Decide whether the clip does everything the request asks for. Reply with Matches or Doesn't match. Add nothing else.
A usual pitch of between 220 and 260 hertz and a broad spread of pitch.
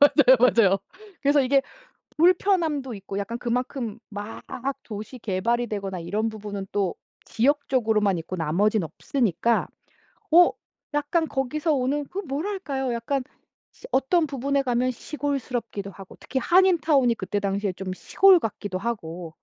Matches